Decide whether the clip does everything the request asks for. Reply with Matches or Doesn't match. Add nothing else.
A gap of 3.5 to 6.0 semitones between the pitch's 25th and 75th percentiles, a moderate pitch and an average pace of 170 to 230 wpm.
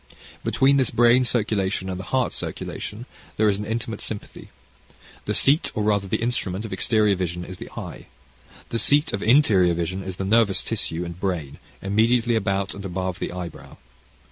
Doesn't match